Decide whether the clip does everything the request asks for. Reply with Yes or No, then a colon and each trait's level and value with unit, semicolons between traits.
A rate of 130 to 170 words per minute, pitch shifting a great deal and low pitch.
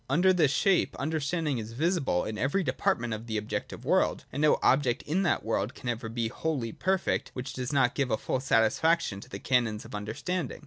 No: average, 195 wpm; wide, 6.0 semitones; low, 130 Hz